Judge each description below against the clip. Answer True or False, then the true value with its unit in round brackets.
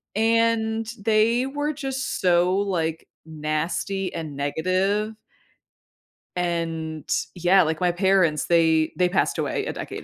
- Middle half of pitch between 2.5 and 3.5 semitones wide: False (5.0 semitones)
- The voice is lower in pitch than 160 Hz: False (185 Hz)